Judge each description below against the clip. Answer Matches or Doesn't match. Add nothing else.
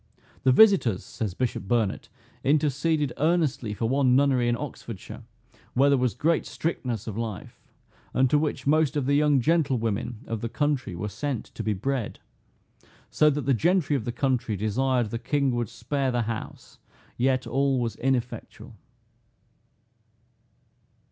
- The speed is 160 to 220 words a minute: Doesn't match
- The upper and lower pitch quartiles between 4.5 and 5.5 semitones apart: Doesn't match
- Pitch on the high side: Doesn't match